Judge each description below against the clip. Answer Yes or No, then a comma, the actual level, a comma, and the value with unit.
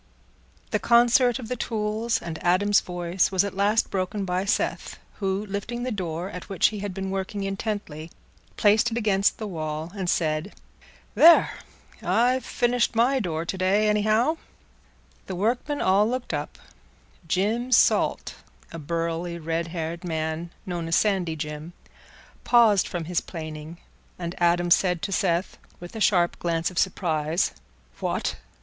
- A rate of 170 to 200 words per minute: No, average, 150 wpm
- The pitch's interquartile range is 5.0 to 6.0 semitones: No, average, 4.1 semitones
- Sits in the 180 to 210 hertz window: Yes, high, 190 Hz